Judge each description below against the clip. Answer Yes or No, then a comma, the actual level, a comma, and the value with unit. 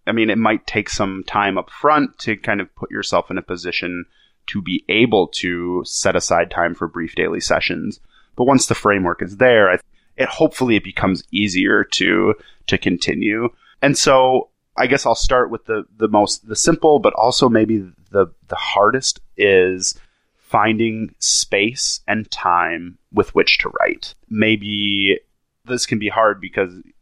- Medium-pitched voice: No, low, 105 Hz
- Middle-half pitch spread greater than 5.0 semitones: No, average, 3.7 semitones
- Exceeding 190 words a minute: No, average, 165 wpm